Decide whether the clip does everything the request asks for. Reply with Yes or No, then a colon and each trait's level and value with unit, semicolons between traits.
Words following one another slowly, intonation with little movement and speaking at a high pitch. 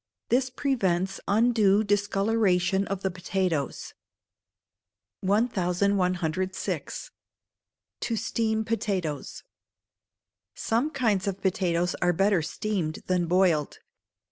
No: slow, 85 wpm; average, 3.4 semitones; high, 195 Hz